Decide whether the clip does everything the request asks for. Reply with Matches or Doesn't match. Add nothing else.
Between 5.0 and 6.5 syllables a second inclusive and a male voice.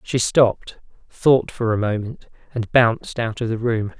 Doesn't match